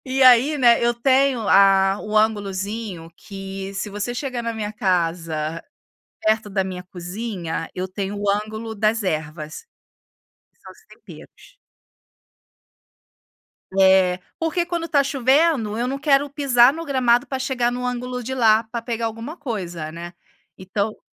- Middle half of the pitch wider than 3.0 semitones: Yes, average, 4.7 semitones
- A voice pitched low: No, high, 220 Hz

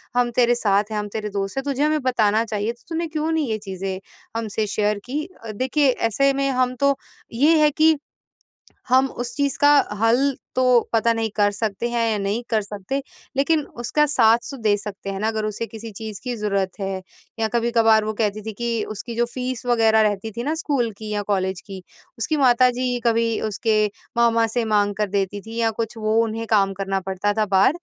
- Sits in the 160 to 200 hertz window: No, high, 225 Hz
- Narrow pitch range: No, average, 3.2 semitones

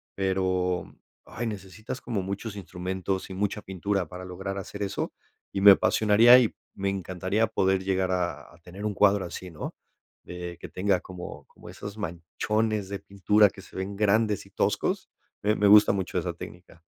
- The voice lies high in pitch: No, very low, 95 Hz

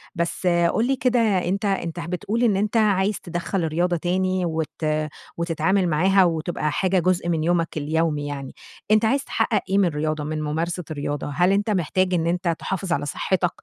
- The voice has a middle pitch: Yes, medium, 175 Hz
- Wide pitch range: No, average, 3.2 semitones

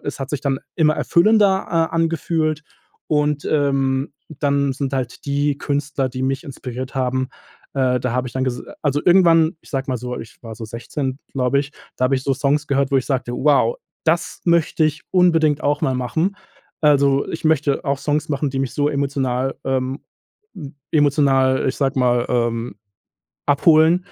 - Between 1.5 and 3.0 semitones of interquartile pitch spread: Yes, narrow, 2.5 semitones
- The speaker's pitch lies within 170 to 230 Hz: No, medium, 140 Hz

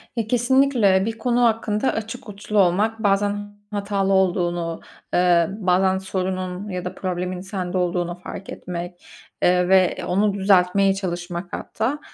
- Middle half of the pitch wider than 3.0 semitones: No, narrow, 2.5 semitones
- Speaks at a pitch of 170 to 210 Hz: Yes, high, 190 Hz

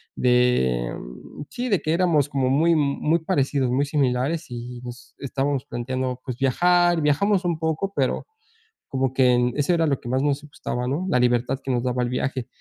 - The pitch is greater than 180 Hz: No, low, 135 Hz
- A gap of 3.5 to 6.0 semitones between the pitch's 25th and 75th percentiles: Yes, average, 4.1 semitones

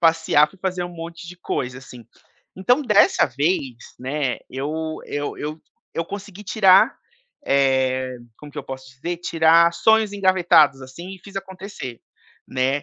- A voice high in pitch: No, medium, 165 Hz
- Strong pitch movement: Yes, wide, 5.8 semitones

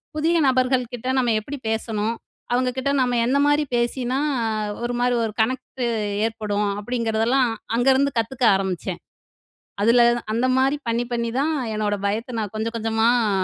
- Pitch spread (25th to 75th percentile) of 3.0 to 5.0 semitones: No, narrow, 2.6 semitones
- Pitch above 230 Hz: Yes, high, 240 Hz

